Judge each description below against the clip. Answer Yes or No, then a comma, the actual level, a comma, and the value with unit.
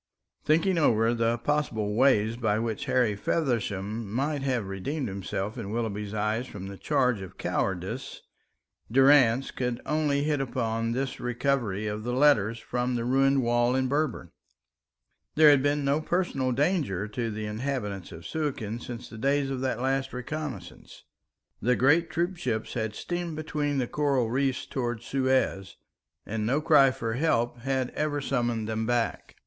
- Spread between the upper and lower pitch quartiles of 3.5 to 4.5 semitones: Yes, average, 3.9 semitones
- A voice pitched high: No, low, 125 Hz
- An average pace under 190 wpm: Yes, average, 155 wpm